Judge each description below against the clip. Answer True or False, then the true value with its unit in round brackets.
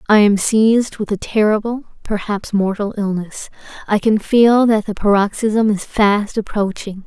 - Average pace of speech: True (155 wpm)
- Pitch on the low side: False (210 Hz)